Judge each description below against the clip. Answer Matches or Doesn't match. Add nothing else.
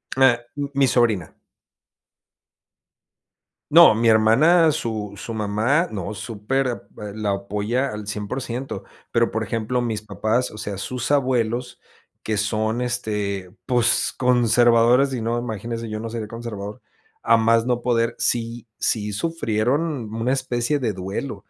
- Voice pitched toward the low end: Matches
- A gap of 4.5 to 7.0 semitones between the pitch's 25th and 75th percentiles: Doesn't match